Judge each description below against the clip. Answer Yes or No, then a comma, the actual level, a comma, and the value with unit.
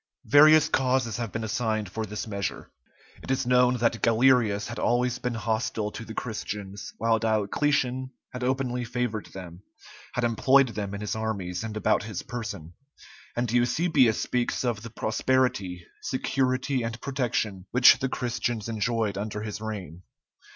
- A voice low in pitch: Yes, low, 115 Hz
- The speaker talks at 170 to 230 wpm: No, average, 150 wpm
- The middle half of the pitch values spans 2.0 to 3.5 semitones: Yes, average, 3.0 semitones